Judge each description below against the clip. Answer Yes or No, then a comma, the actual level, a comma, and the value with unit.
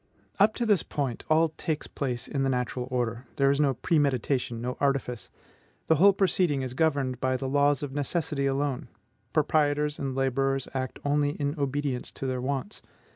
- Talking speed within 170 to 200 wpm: Yes, average, 175 wpm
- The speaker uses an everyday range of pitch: No, narrow, 2.3 semitones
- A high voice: No, medium, 140 Hz